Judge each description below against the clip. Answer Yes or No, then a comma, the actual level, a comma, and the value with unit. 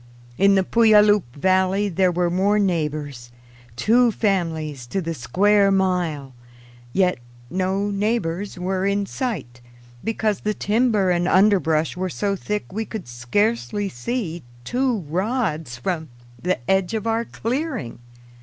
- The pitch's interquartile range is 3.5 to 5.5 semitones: Yes, average, 4.2 semitones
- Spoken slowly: Yes, slow, 130 wpm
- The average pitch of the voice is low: No, high, 190 Hz